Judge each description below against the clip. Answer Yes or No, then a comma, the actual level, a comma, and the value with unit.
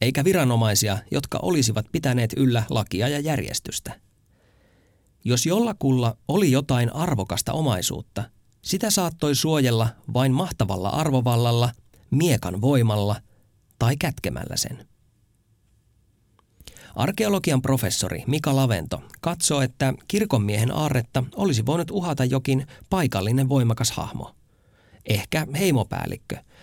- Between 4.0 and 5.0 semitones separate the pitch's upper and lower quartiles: Yes, average, 4.7 semitones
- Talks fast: No, slow, 95 wpm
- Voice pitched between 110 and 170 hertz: Yes, low, 125 Hz